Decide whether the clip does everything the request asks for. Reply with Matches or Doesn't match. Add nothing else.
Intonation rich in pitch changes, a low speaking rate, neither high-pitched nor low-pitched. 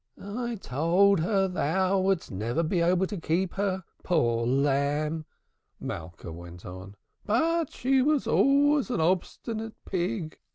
Matches